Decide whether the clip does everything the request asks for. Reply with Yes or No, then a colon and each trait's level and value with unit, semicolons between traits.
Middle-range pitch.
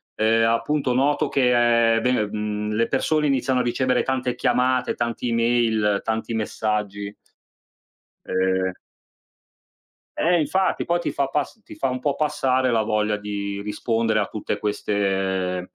No: low, 115 Hz